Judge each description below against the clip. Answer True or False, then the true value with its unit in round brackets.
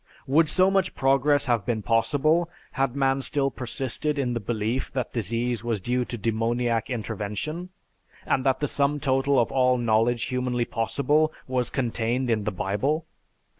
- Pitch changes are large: False (3.4 semitones)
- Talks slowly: False (160 wpm)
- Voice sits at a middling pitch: False (125 Hz)